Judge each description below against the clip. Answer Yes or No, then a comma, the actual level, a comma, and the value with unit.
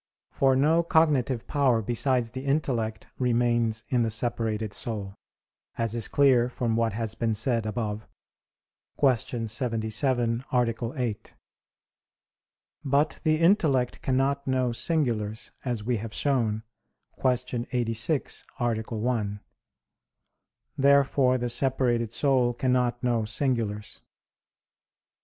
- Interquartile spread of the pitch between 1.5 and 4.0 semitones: Yes, average, 2.8 semitones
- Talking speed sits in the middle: No, slow, 110 wpm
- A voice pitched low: Yes, low, 120 Hz